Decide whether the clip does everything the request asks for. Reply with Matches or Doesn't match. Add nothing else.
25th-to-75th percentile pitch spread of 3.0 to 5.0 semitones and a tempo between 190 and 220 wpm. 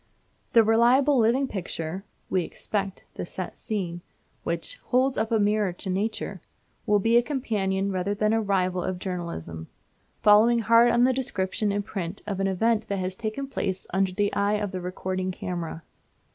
Doesn't match